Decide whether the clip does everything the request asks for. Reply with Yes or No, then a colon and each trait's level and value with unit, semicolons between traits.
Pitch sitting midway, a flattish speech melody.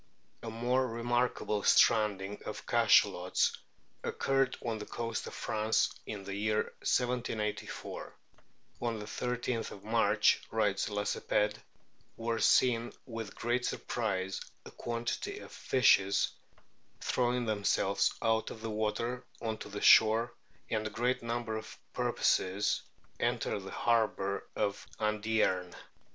No: low, 110 Hz; narrow, 2.1 semitones